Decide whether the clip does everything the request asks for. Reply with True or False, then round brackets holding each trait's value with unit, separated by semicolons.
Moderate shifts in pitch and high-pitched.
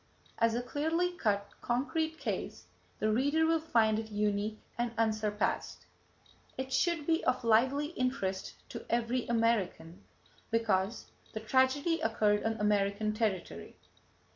True (4.2 semitones; 230 Hz)